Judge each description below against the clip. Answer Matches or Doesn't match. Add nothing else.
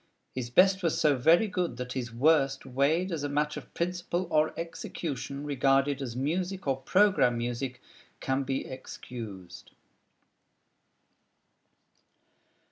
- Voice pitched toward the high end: Doesn't match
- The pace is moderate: Doesn't match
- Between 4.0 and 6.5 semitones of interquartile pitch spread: Matches